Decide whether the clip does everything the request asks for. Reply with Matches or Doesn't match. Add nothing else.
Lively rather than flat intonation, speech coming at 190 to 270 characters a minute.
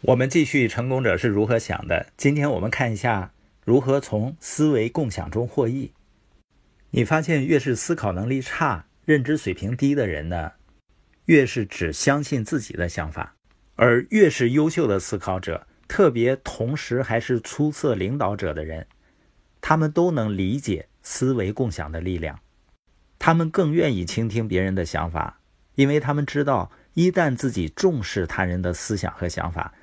Matches